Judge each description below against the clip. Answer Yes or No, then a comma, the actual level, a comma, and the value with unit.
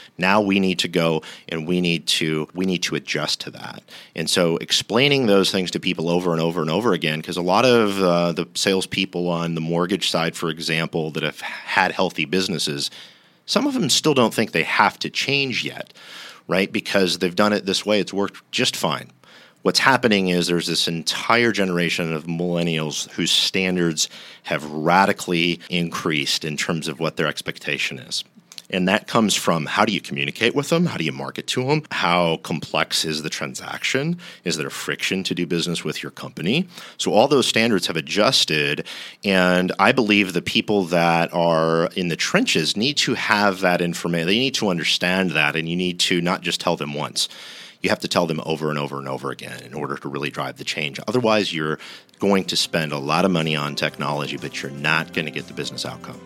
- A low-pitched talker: Yes, very low, 85 Hz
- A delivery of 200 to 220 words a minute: Yes, fast, 205 wpm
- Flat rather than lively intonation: No, average, 3.3 semitones